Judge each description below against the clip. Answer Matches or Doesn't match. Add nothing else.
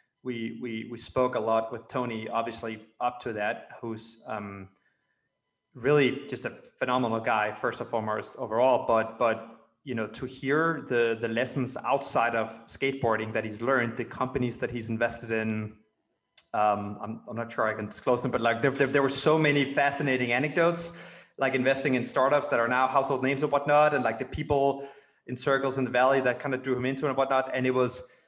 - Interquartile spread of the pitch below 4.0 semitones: Matches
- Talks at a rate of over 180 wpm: Matches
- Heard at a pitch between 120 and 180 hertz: Matches